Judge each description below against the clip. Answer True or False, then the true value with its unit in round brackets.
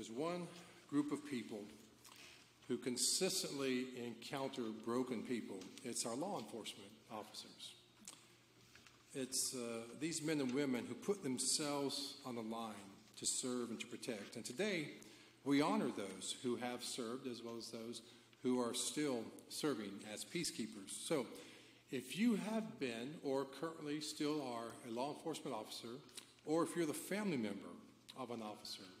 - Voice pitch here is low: True (125 Hz)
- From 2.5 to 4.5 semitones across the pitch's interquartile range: True (3.8 semitones)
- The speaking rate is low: False (150 wpm)